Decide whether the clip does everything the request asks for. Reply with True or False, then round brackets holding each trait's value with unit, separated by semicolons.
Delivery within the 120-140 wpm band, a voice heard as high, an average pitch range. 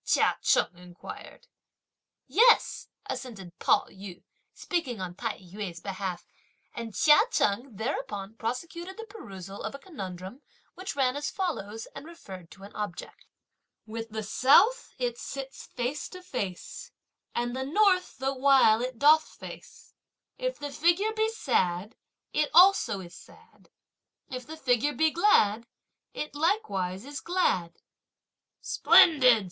False (135 wpm; 255 Hz; 8.0 semitones)